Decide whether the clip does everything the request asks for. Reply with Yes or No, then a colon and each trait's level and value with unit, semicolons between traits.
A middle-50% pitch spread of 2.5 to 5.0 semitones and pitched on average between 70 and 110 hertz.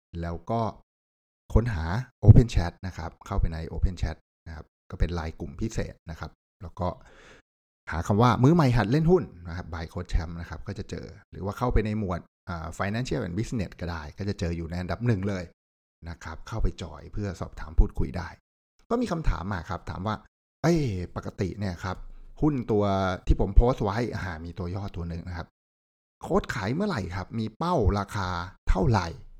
Yes: average, 4.2 semitones; very low, 90 Hz